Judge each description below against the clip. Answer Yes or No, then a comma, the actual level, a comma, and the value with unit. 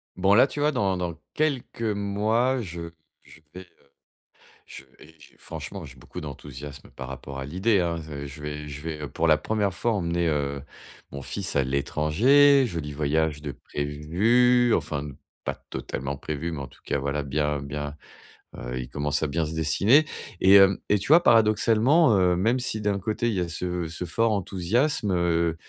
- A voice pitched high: No, very low, 85 Hz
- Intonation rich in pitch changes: Yes, wide, 6.5 semitones